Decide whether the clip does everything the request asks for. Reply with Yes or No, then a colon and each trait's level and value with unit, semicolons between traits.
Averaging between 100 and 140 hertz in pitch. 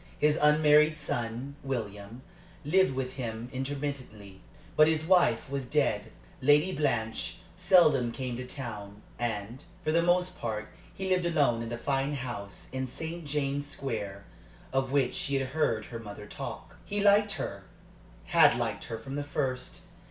Yes: low, 135 Hz